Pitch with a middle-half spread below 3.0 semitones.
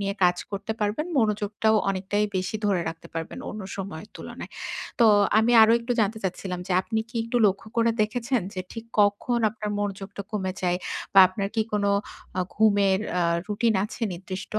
Yes: narrow, 2.4 semitones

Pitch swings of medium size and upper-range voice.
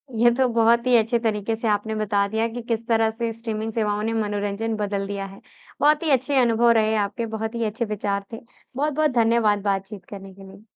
No: narrow, 2.2 semitones; high, 220 Hz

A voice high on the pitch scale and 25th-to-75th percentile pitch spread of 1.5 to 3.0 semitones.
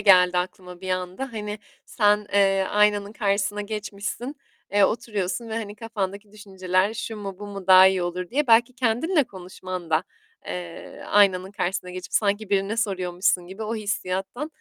Yes: high, 200 Hz; narrow, 2.5 semitones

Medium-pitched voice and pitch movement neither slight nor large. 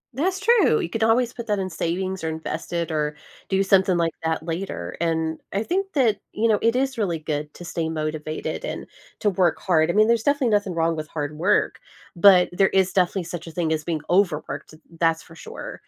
Yes: medium, 175 Hz; average, 4.5 semitones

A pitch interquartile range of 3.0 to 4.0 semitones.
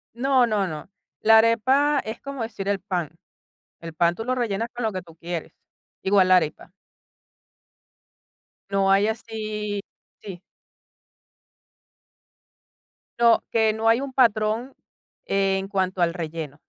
Yes: average, 3.7 semitones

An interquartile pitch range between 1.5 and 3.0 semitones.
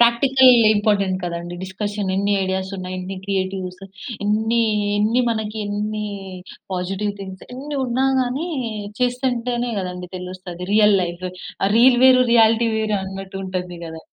No: average, 4.0 semitones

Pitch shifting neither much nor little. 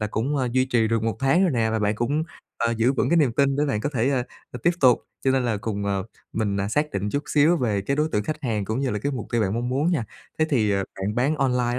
Yes: average, 4.3 semitones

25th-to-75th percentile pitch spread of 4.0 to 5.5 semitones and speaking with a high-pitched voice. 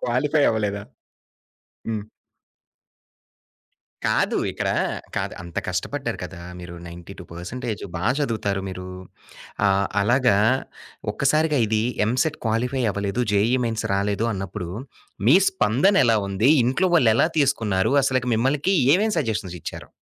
No: average, 5.0 semitones; low, 115 Hz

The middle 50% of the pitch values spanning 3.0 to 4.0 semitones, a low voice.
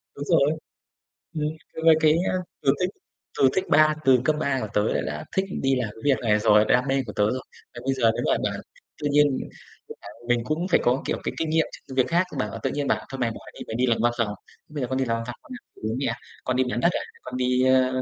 Yes: average, 3.7 semitones; low, 130 Hz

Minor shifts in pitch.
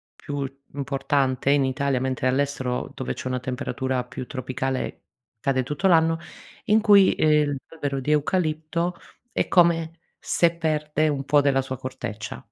No: average, 3.2 semitones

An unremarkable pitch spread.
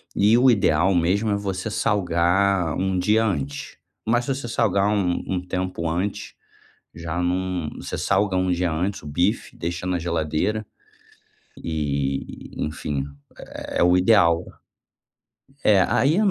Yes: average, 3.3 semitones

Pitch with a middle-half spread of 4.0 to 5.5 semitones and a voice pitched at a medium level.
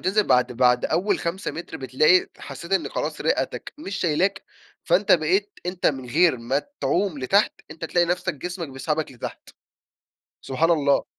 Yes: average, 5.2 semitones; medium, 165 Hz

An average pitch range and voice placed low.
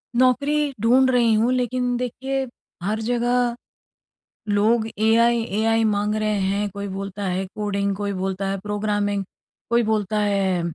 No: average, 3.1 semitones; high, 215 Hz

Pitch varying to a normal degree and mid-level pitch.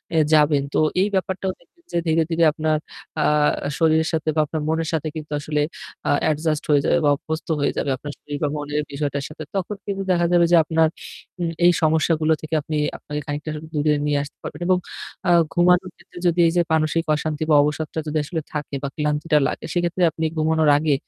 No: narrow, 1.8 semitones; medium, 155 Hz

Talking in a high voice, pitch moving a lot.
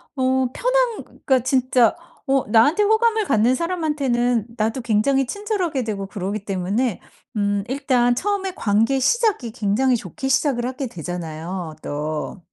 Yes: very high, 250 Hz; wide, 5.9 semitones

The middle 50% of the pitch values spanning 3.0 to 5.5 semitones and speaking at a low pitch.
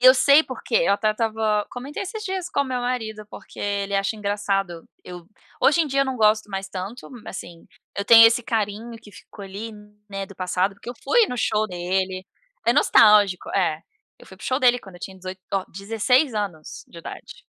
No: average, 4.2 semitones; high, 210 Hz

